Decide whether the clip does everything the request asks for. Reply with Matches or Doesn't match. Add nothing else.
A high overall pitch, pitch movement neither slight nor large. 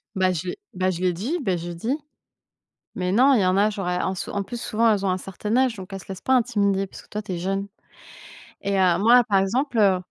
Matches